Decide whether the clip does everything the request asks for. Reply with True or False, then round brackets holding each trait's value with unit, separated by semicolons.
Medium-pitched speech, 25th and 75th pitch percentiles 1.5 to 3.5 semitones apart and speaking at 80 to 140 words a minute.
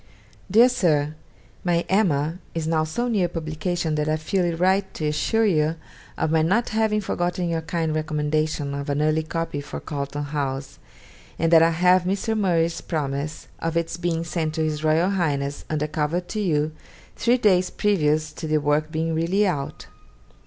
False (160 Hz; 2.9 semitones; 175 wpm)